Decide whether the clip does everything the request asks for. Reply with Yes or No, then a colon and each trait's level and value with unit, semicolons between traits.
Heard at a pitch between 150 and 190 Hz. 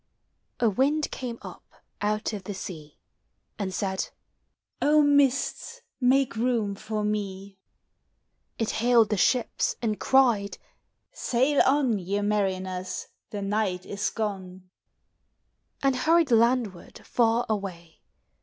No: high, 215 Hz